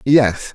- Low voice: Yes, low, 125 Hz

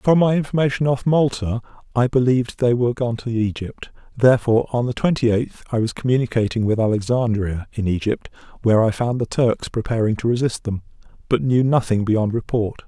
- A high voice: No, low, 115 Hz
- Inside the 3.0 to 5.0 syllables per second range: No, 5.7 syllables/s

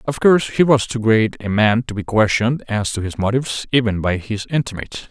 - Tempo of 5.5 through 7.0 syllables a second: Yes, 5.8 syllables/s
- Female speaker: No, male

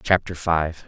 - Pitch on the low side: Yes, very low, 85 Hz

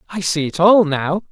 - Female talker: No, male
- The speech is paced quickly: Yes, fast, 230 wpm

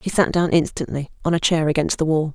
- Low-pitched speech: No, medium, 160 Hz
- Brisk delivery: Yes, fast, 255 wpm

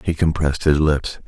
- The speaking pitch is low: Yes, very low, 75 Hz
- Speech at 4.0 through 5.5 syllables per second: Yes, 5.3 syllables/s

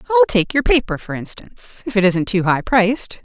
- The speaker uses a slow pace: No, fast, 205 wpm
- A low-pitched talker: No, high, 200 Hz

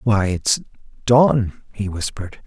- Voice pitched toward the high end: No, low, 110 Hz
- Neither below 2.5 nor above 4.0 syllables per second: Yes, 3.8 syllables/s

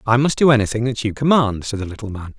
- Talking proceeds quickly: Yes, fast, 275 wpm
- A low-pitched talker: Yes, low, 115 Hz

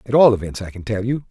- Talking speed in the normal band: No, fast, 320 wpm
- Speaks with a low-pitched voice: Yes, low, 115 Hz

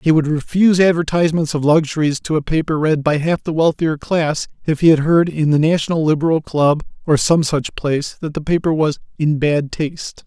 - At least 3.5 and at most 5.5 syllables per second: Yes, 5.4 syllables/s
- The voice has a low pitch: No, medium, 155 Hz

